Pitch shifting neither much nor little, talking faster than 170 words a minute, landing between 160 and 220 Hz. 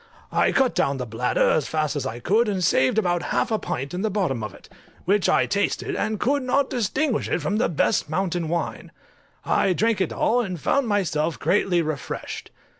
No: wide, 6.0 semitones; average, 200 wpm; medium, 185 Hz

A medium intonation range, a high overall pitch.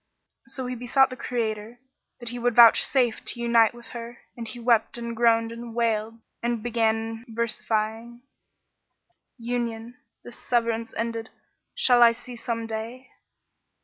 No: narrow, 1.1 semitones; high, 235 Hz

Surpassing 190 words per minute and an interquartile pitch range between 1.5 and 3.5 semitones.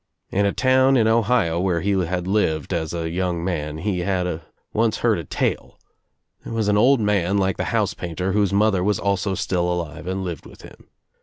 Yes: fast, 205 wpm; average, 3.2 semitones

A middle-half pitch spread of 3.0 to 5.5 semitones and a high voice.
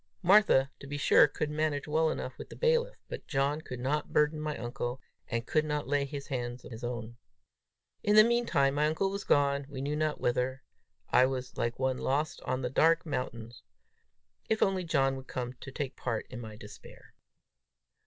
No: average, 3.3 semitones; medium, 140 Hz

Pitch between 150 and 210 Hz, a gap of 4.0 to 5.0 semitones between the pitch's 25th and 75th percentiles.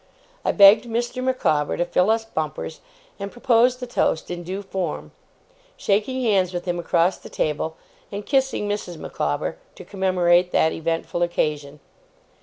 Yes: high, 190 Hz; average, 4.5 semitones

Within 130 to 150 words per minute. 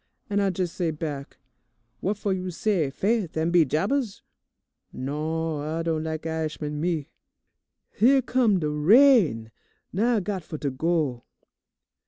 Yes: average, 145 wpm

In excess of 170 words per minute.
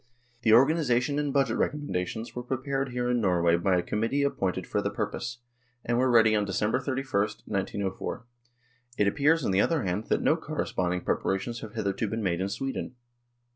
Yes: average, 180 wpm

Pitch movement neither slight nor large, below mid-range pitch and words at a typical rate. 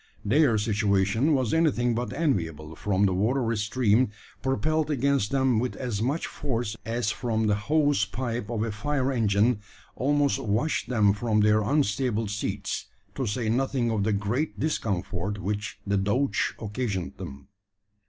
Yes: average, 4.4 semitones; low, 115 Hz; average, 150 wpm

